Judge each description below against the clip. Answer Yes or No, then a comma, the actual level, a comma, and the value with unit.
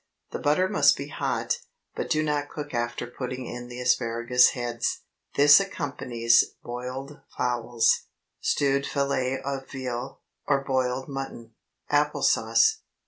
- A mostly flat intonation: No, average, 3.0 semitones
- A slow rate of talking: Yes, slow, 130 wpm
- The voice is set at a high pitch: No, low, 130 Hz